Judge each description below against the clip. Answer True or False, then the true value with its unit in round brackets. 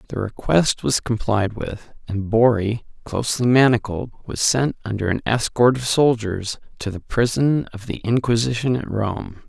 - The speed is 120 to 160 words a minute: True (150 wpm)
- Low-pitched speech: True (115 Hz)